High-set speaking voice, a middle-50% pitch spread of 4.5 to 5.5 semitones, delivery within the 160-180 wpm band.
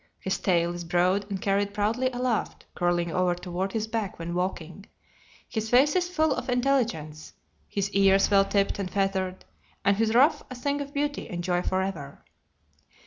Yes: high, 195 Hz; average, 5.1 semitones; average, 175 wpm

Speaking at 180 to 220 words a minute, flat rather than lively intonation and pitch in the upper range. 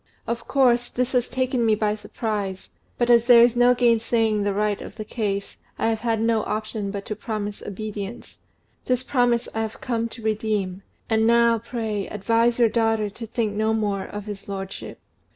Yes: average, 190 wpm; narrow, 2.1 semitones; high, 220 Hz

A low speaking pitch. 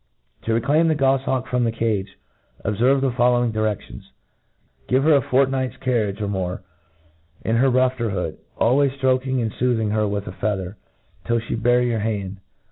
Yes: low, 120 Hz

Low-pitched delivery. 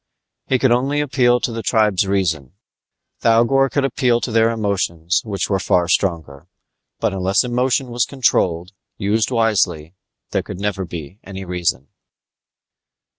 Yes: low, 105 Hz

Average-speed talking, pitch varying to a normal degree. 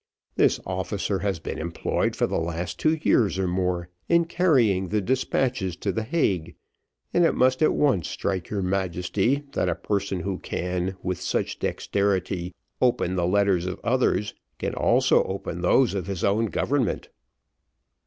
Yes: average, 160 wpm; average, 4.2 semitones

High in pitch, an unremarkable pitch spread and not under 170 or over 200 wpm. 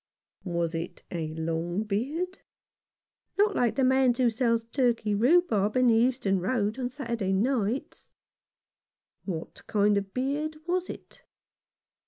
No: high, 230 Hz; average, 4.9 semitones; average, 160 wpm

